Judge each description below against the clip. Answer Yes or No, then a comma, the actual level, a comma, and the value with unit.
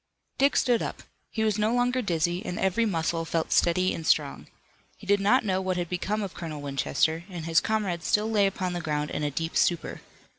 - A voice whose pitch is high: No, medium, 180 Hz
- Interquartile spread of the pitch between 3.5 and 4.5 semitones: Yes, average, 4.2 semitones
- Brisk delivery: Yes, fast, 215 wpm